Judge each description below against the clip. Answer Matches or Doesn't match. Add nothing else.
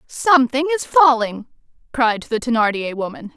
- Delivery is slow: Matches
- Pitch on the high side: Matches